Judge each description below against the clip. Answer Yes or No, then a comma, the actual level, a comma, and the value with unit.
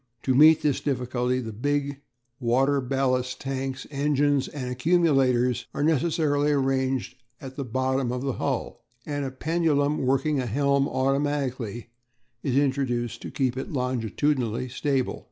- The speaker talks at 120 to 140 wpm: Yes, slow, 135 wpm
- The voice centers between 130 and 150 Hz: Yes, low, 135 Hz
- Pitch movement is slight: Yes, narrow, 2.1 semitones